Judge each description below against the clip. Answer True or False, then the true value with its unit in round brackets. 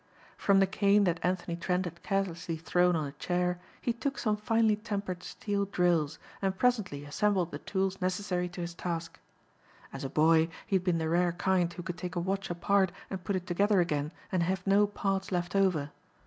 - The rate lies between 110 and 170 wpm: False (200 wpm)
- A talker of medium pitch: True (180 Hz)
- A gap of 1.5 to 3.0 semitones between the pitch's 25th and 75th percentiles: True (2.4 semitones)